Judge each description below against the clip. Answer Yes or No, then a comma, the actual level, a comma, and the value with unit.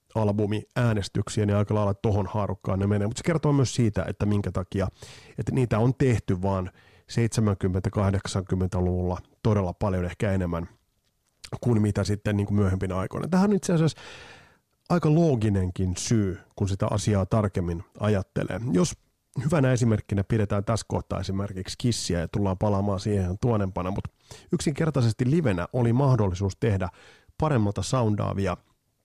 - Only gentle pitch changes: No, average, 3.5 semitones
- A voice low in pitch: Yes, low, 105 Hz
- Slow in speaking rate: No, average, 135 wpm